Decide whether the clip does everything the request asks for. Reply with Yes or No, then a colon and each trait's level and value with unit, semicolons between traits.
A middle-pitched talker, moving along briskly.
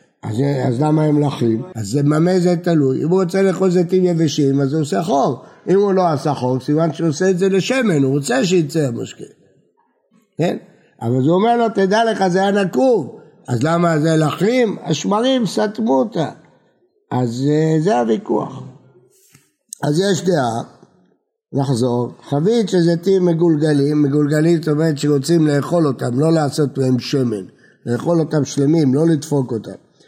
Yes: medium, 155 Hz; fast, 160 wpm